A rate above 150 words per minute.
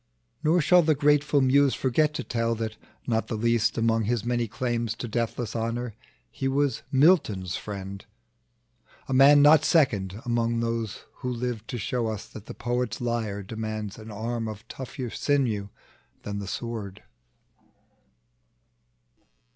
No: average, 145 wpm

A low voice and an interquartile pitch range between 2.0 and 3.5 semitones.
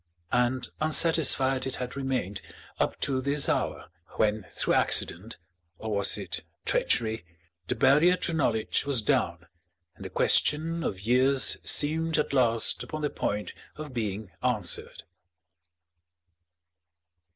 No: low, 130 Hz; average, 5.1 semitones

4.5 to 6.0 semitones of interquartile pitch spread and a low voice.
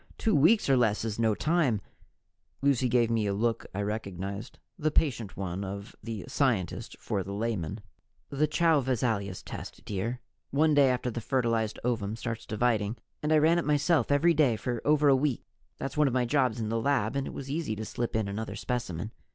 Yes: average, 4.8 semitones; low, 120 Hz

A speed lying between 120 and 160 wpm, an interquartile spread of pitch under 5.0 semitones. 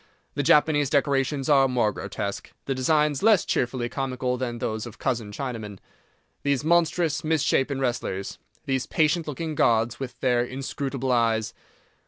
Yes: average, 145 wpm; average, 3.4 semitones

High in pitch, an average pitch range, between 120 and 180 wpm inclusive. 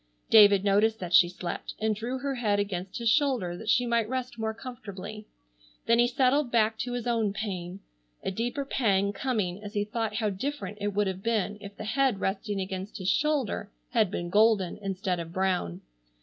No: high, 210 Hz; average, 3.5 semitones; average, 190 wpm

